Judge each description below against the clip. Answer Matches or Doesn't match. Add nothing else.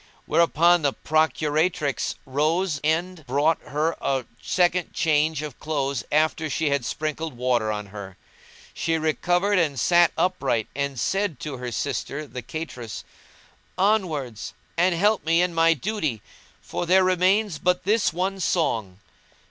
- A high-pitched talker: Doesn't match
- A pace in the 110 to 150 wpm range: Matches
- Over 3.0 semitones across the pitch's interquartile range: Matches